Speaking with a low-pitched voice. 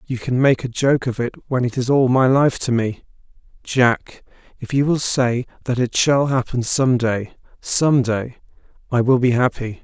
Yes: low, 125 Hz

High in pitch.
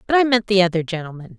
Yes: high, 195 Hz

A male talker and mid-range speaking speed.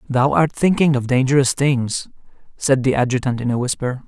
Yes: male; average, 175 wpm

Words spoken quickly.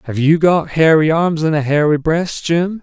Yes: fast, 215 wpm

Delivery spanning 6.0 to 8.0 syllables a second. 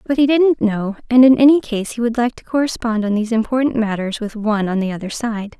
Yes: 6.1 syllables/s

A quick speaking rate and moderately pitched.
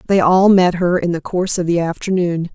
Yes: fast, 235 wpm; medium, 175 Hz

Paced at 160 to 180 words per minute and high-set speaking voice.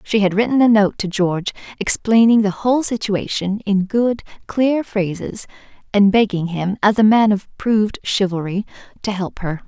Yes: average, 165 wpm; high, 205 Hz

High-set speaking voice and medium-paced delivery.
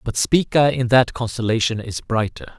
No: low, 120 Hz; average, 160 wpm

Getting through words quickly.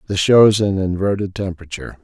No: average, 145 wpm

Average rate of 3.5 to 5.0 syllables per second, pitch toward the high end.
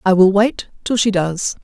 Yes: 4.4 syllables/s; high, 200 Hz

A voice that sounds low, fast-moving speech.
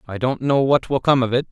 Yes: low, 130 Hz; fast, 315 wpm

